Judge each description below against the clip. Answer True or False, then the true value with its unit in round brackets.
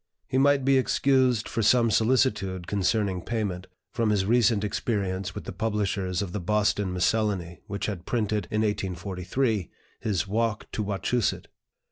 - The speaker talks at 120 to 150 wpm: True (145 wpm)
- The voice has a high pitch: False (105 Hz)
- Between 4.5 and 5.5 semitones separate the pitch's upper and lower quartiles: False (3.3 semitones)